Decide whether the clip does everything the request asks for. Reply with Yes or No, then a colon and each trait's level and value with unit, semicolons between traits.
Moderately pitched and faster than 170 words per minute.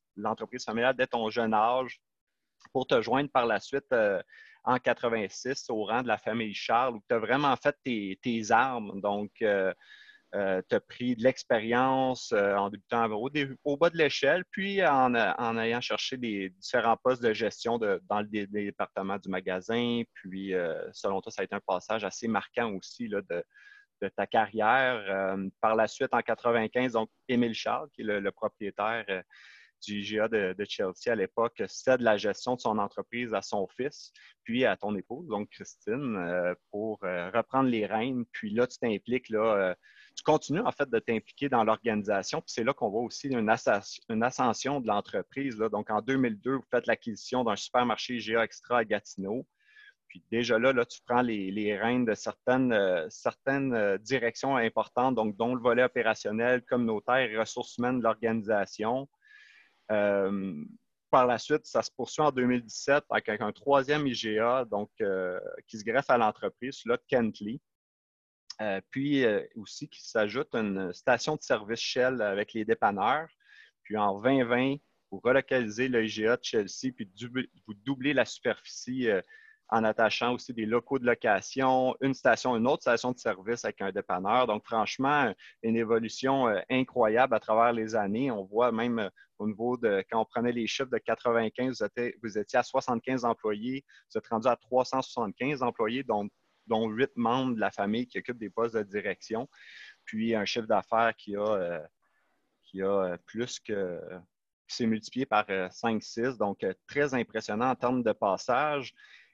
No: low, 120 Hz; average, 180 wpm